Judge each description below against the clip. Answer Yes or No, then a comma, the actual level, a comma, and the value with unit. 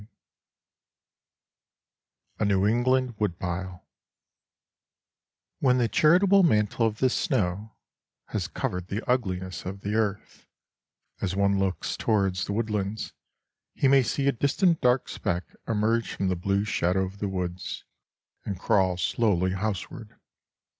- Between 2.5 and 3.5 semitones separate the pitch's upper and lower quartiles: No, average, 4.1 semitones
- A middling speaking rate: No, slow, 125 wpm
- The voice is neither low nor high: No, low, 105 Hz